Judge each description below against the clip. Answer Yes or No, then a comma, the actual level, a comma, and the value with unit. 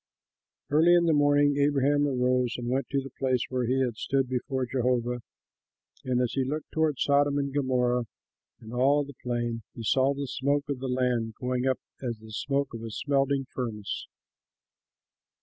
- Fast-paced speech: No, average, 175 wpm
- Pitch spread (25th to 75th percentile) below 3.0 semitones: Yes, narrow, 2.4 semitones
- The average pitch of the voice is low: Yes, low, 130 Hz